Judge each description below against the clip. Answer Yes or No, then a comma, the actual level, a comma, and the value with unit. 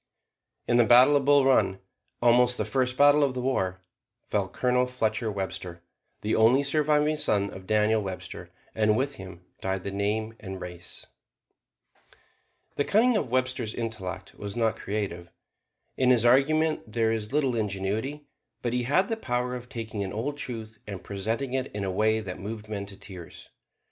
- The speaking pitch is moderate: No, low, 115 Hz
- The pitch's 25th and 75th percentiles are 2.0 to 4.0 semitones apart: No, average, 4.4 semitones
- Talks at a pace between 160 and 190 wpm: Yes, average, 170 wpm